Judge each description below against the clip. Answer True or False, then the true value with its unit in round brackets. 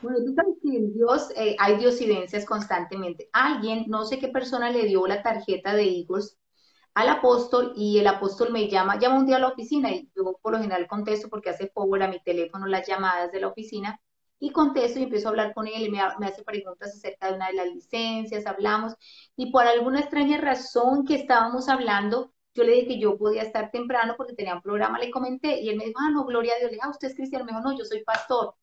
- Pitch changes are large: False (3.8 semitones)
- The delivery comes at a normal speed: False (230 wpm)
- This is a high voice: True (220 Hz)